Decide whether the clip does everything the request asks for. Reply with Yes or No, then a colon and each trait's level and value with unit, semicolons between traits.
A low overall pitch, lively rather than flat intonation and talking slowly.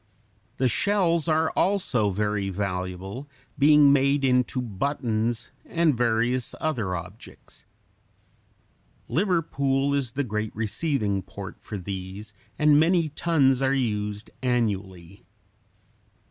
Yes: low, 125 Hz; wide, 5.7 semitones; slow, 105 wpm